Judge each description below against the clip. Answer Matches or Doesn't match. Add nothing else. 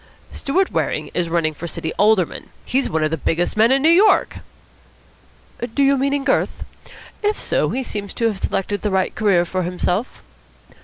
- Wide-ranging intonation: Matches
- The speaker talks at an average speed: Matches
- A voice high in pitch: Matches